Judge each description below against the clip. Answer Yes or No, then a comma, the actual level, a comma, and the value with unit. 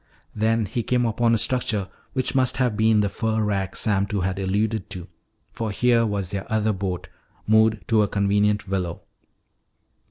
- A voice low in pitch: Yes, low, 105 Hz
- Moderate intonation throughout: No, narrow, 2.3 semitones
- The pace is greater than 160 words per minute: Yes, average, 170 wpm